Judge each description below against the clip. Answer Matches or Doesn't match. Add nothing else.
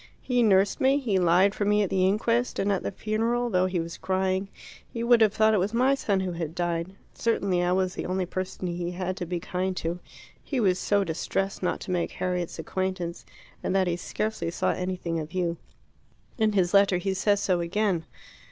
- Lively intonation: Doesn't match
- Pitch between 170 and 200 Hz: Matches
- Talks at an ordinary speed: Doesn't match